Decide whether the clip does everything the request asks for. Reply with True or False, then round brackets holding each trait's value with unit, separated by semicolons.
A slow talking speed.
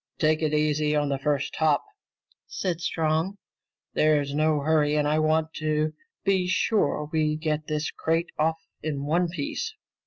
False (155 wpm)